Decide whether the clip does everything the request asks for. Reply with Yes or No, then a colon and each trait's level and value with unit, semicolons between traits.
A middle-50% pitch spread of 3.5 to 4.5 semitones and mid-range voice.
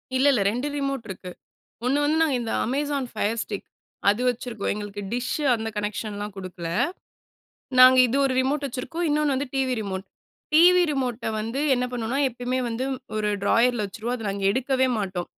No: average, 4.2 semitones; high, 245 Hz